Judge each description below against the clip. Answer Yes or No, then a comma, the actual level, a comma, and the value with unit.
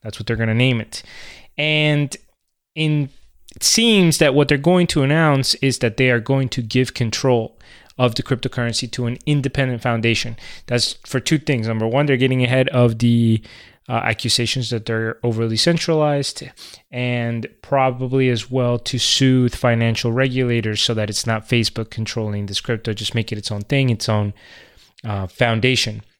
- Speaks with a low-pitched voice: Yes, low, 120 Hz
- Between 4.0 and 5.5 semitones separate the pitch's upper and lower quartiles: No, average, 2.9 semitones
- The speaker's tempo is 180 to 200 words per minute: No, average, 170 wpm